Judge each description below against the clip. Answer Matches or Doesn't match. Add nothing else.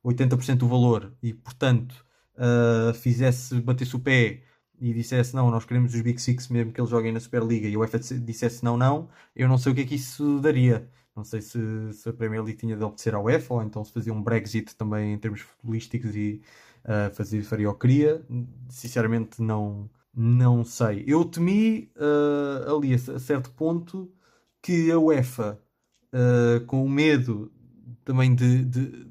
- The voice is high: Doesn't match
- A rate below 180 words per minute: Doesn't match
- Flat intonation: Matches